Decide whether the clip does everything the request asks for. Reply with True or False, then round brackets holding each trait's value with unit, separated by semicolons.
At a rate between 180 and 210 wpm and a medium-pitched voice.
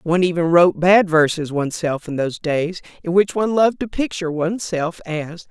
True (185 wpm; 170 Hz)